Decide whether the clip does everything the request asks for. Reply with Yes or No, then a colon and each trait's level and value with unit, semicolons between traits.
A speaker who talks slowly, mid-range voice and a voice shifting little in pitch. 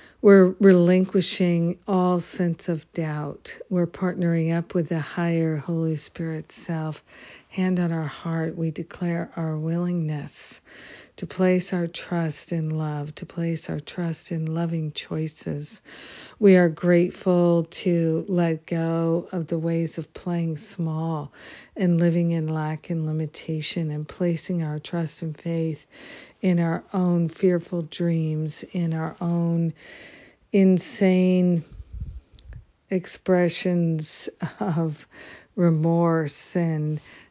Yes: slow, 115 wpm; medium, 170 Hz; narrow, 1.8 semitones